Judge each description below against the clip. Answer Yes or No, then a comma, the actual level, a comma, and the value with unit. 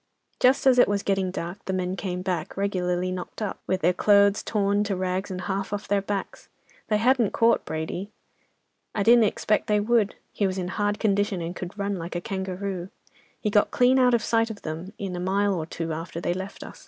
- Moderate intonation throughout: No, narrow, 2.3 semitones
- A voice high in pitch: Yes, high, 195 Hz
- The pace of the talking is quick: Yes, fast, 215 wpm